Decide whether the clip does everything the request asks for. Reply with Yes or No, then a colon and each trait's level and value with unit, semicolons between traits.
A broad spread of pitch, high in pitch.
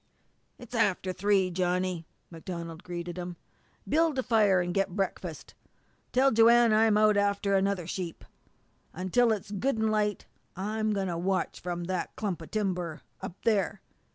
No: average, 3.3 semitones; high, 195 Hz